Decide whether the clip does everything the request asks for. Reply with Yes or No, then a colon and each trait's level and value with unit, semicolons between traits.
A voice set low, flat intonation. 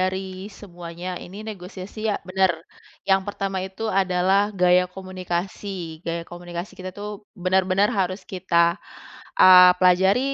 No: medium, 185 Hz; narrow, 1.3 semitones